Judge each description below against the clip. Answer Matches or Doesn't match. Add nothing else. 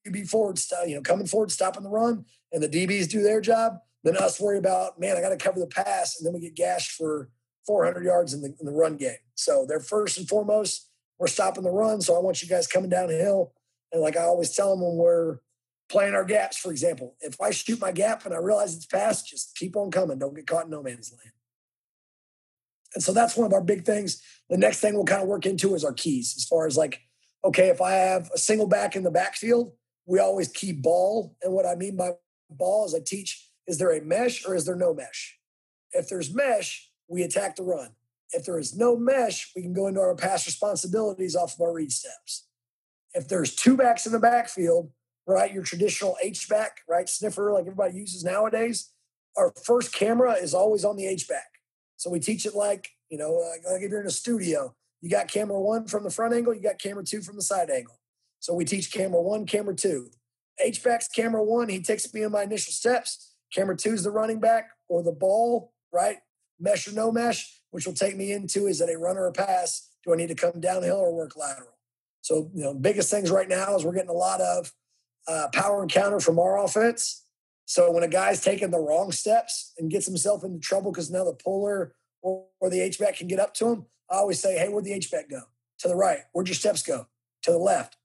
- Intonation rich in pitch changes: Doesn't match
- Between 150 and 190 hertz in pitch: Matches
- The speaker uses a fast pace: Matches